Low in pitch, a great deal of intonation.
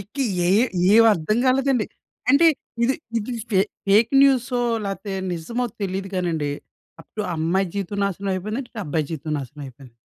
No: high, 195 Hz; wide, 5.8 semitones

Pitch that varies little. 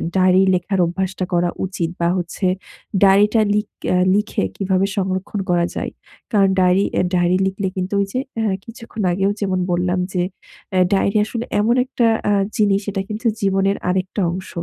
Yes: narrow, 1.9 semitones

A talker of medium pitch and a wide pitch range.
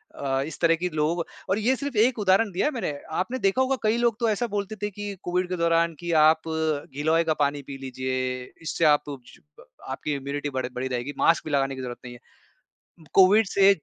Yes: medium, 165 Hz; wide, 6.1 semitones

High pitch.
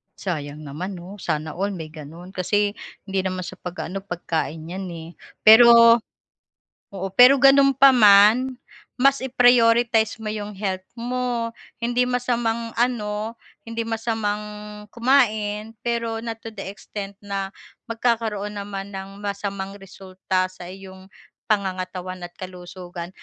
Yes: high, 205 Hz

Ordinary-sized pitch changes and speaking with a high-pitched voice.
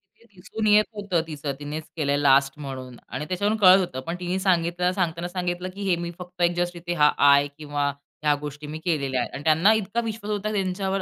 No: average, 4.4 semitones; medium, 175 Hz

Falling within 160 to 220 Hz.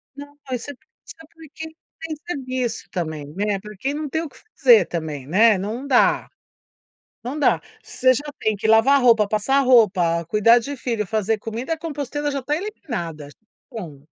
No: high, 235 Hz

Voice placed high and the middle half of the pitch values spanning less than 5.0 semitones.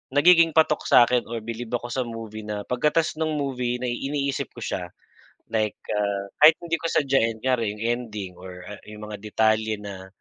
No: low, 115 Hz; average, 4.4 semitones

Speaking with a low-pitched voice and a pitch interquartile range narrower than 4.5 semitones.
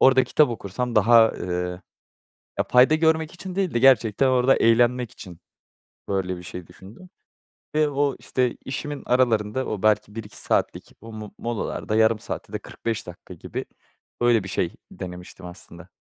No: low, 115 Hz; average, 5.3 semitones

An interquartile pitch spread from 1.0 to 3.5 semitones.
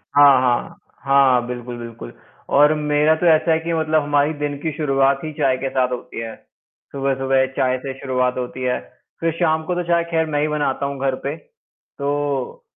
Yes: average, 2.9 semitones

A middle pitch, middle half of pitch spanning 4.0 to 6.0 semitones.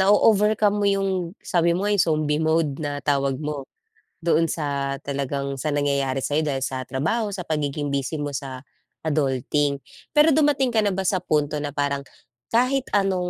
Yes: medium, 155 Hz; wide, 5.6 semitones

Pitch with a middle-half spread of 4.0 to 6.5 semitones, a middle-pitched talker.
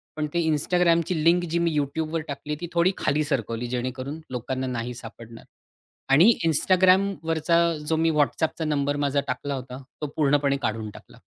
Yes: average, 4.3 semitones; medium, 145 Hz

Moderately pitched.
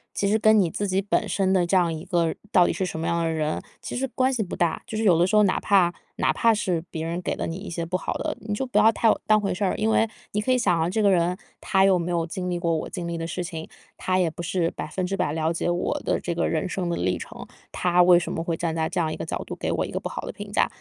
Yes: medium, 180 Hz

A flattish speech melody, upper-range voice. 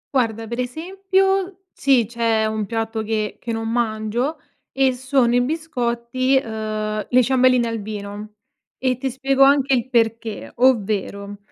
No: average, 3.4 semitones; high, 235 Hz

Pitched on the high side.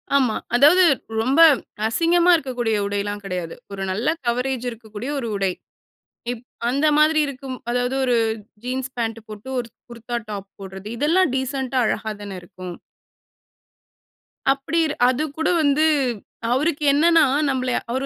Yes: very high, 250 Hz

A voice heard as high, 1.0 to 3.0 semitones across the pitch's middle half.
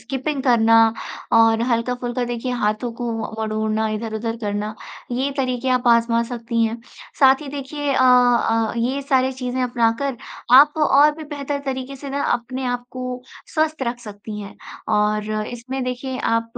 Yes: high, 245 Hz; narrow, 2.6 semitones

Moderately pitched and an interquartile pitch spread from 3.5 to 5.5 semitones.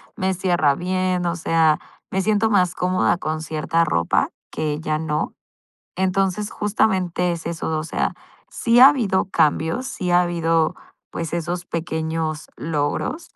No: medium, 170 Hz; average, 2.8 semitones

